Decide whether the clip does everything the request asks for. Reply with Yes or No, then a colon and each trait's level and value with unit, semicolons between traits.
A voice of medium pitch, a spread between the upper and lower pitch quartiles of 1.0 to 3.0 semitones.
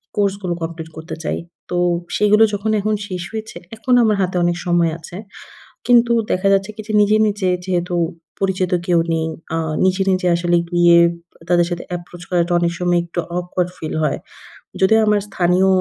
Yes: medium, 180 Hz; average, 2.7 semitones